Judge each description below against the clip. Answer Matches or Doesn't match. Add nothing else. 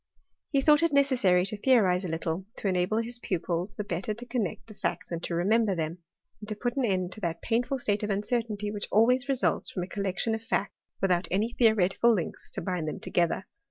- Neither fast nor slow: Doesn't match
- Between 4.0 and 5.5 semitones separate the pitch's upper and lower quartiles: Matches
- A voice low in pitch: Doesn't match